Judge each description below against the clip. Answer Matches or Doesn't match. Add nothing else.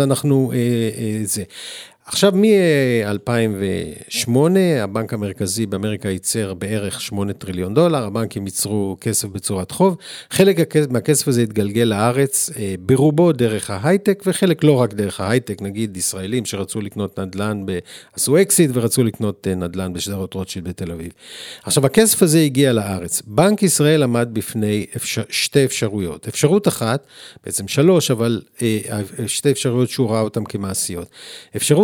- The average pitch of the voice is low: Matches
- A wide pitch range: Matches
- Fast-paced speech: Doesn't match